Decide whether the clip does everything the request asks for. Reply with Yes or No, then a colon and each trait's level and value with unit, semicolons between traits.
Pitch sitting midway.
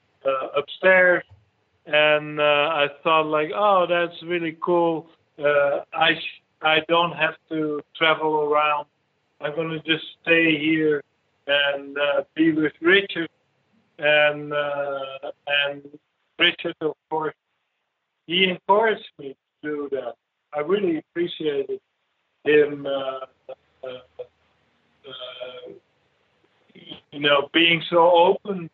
Yes: medium, 155 Hz